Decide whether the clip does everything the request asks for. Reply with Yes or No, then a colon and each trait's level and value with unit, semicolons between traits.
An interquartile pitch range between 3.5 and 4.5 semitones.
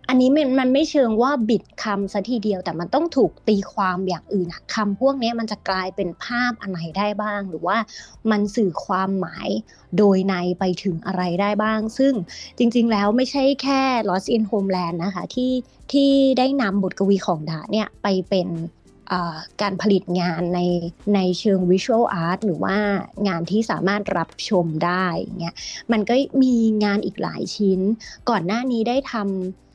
Yes: average, 3.9 semitones